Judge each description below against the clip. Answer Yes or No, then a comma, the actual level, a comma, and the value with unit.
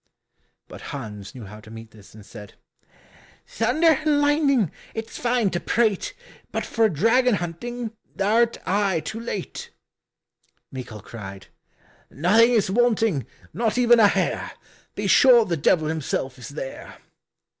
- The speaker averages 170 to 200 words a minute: No, slow, 135 wpm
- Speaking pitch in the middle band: No, high, 205 Hz